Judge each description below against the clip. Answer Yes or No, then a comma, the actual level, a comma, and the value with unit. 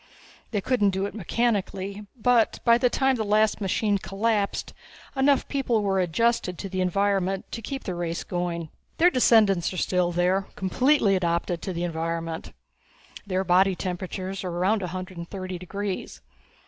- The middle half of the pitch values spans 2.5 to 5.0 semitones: Yes, average, 3.3 semitones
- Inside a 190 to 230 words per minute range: No, average, 160 wpm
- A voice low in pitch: No, high, 195 Hz